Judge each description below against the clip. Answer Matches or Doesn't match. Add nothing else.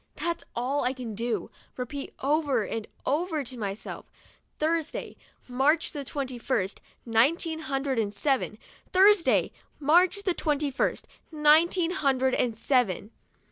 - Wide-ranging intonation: Doesn't match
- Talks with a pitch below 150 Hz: Doesn't match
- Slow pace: Matches